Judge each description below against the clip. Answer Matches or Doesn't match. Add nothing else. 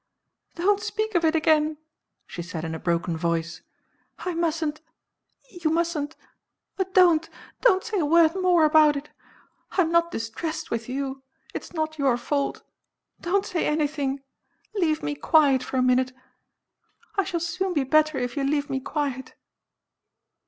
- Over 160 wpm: Doesn't match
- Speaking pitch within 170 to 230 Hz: Doesn't match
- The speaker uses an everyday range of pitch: Matches